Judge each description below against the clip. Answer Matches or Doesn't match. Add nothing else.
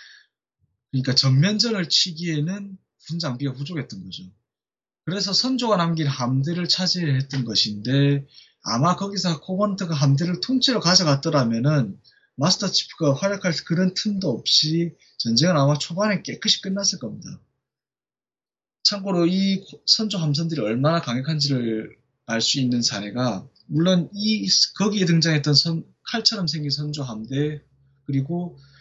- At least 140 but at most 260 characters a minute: Doesn't match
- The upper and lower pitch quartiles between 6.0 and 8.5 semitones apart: Doesn't match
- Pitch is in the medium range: Matches